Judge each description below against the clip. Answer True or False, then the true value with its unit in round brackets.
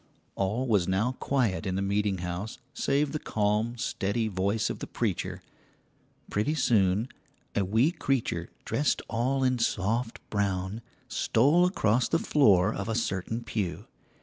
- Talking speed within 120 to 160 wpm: True (145 wpm)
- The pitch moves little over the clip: False (4.4 semitones)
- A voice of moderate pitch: False (110 Hz)